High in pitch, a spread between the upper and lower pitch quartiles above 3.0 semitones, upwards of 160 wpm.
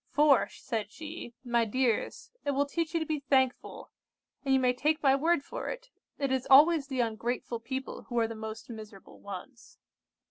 Yes: very high, 265 Hz; average, 3.9 semitones; average, 185 wpm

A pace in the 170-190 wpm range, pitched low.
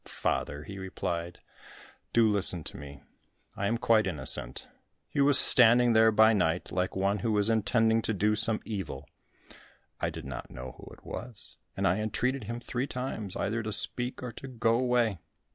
Yes: average, 180 wpm; low, 110 Hz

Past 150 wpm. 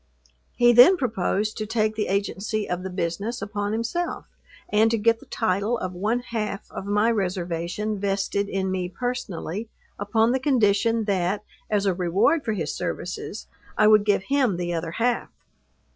Yes: average, 165 wpm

